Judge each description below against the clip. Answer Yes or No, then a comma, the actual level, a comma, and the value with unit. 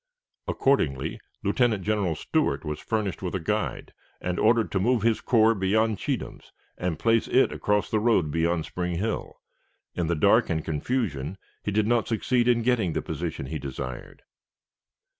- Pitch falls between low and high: No, low, 105 Hz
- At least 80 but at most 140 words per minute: No, average, 160 wpm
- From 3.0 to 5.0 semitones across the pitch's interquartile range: No, wide, 5.4 semitones